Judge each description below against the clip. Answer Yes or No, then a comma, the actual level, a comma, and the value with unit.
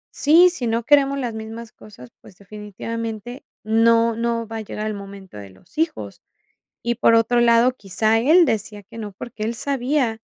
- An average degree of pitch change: No, narrow, 2.3 semitones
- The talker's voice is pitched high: Yes, high, 230 Hz